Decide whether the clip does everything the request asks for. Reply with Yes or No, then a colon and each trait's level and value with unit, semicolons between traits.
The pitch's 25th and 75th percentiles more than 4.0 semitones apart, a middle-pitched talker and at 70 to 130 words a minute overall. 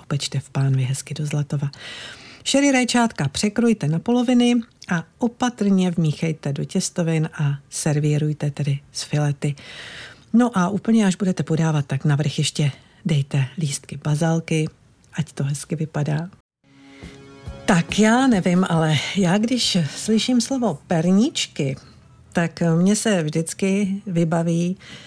Yes: average, 5.1 semitones; medium, 165 Hz; average, 120 wpm